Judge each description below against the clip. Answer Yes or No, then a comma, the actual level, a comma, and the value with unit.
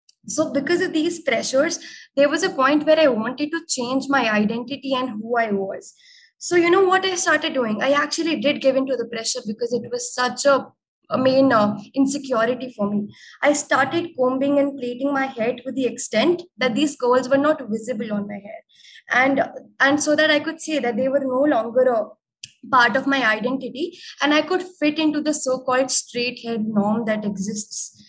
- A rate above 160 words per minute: Yes, average, 200 wpm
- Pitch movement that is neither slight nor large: Yes, average, 3.8 semitones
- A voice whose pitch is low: No, very high, 265 Hz